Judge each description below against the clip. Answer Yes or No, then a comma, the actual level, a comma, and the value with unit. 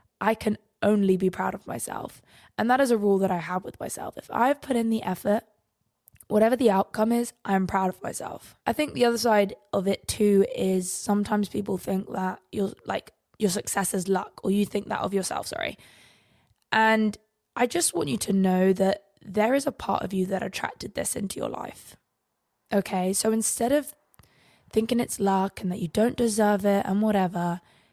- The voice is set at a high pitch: Yes, high, 205 Hz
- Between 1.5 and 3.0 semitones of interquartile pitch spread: Yes, narrow, 2.5 semitones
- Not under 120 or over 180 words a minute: No, average, 200 wpm